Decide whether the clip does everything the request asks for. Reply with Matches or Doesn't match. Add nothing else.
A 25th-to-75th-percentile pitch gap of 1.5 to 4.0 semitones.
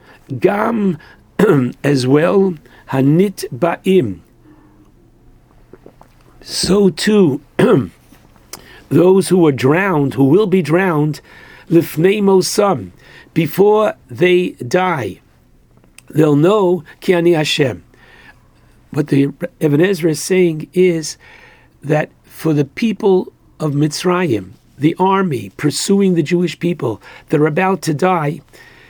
Doesn't match